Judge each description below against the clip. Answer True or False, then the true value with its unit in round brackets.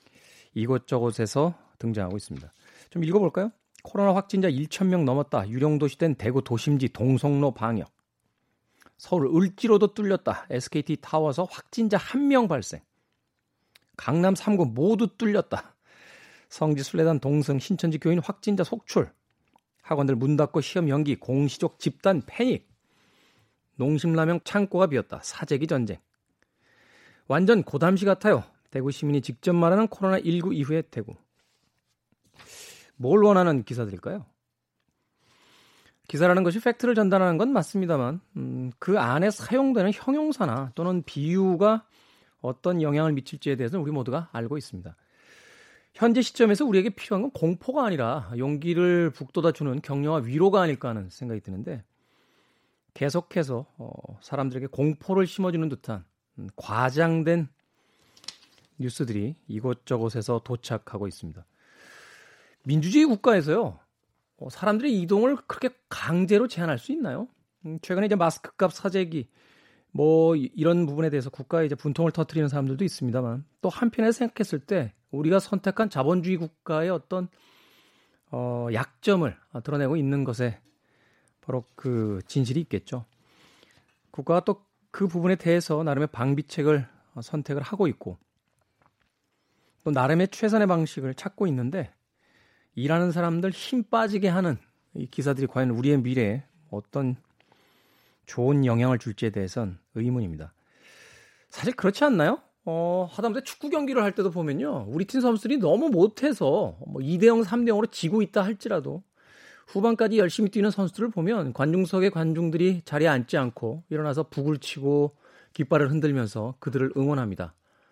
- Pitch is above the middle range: False (160 Hz)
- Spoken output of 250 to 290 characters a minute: False (310 characters per minute)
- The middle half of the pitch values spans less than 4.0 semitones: False (6.5 semitones)